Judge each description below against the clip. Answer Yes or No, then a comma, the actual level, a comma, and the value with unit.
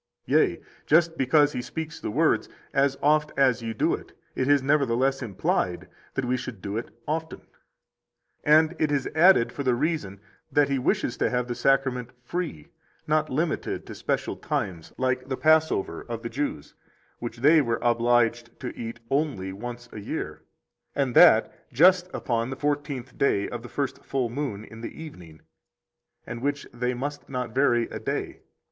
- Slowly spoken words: No, average, 170 wpm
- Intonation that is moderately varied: Yes, average, 3.8 semitones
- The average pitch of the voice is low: Yes, low, 130 Hz